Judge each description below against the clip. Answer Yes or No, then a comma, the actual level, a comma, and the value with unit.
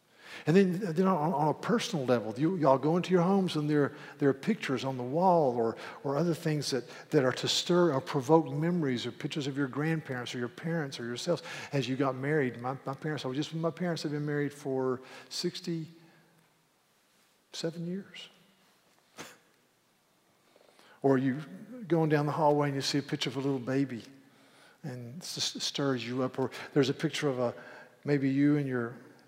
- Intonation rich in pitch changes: No, average, 3.8 semitones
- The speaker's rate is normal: Yes, average, 185 wpm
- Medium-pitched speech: Yes, medium, 145 Hz